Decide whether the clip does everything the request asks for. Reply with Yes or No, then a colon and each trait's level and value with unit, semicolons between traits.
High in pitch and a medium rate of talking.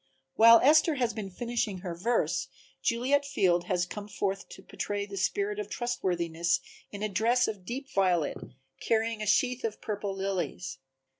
Yes: high, 205 Hz; average, 160 wpm